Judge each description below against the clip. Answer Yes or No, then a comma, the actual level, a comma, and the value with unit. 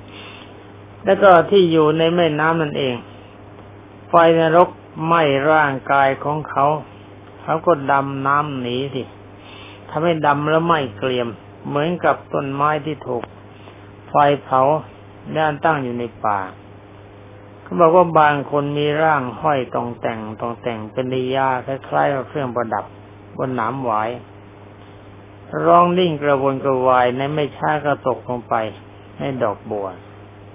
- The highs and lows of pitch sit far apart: Yes, wide, 6.5 semitones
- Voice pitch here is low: Yes, low, 125 Hz